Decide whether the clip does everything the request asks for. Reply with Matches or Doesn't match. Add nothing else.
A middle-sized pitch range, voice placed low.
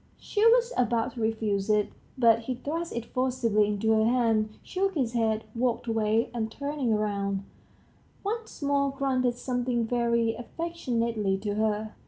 Doesn't match